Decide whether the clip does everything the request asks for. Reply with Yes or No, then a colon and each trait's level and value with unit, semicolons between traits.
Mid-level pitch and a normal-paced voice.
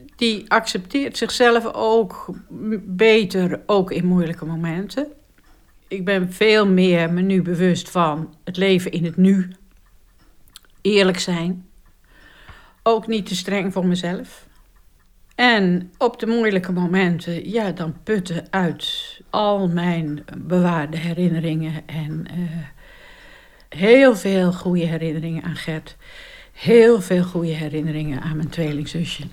No: medium, 180 Hz; slow, 120 wpm